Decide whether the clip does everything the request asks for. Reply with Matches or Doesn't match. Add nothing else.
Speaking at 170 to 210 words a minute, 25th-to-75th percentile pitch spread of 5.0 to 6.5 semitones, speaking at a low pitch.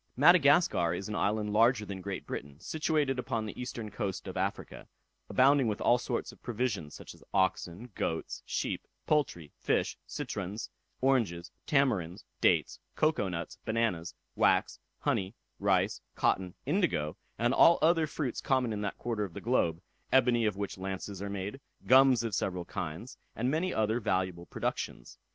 Doesn't match